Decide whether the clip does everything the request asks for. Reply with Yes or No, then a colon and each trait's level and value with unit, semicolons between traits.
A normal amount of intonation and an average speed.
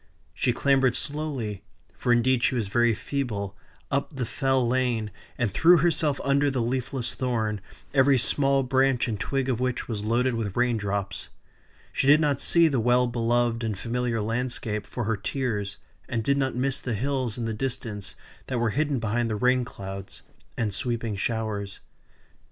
Yes: average, 3.2 semitones; average, 170 wpm